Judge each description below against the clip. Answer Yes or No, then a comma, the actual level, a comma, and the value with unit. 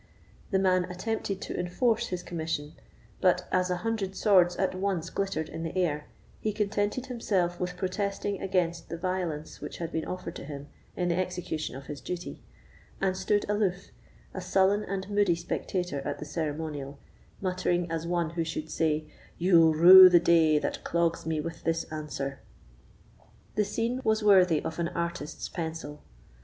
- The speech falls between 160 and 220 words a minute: Yes, average, 165 wpm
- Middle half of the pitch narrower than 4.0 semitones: Yes, average, 2.9 semitones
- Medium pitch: Yes, medium, 175 Hz